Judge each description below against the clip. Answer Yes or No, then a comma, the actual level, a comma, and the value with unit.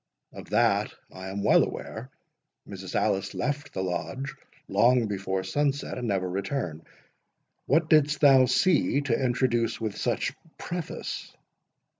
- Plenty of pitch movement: Yes, wide, 6.4 semitones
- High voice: No, low, 125 Hz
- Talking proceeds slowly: Yes, slow, 130 wpm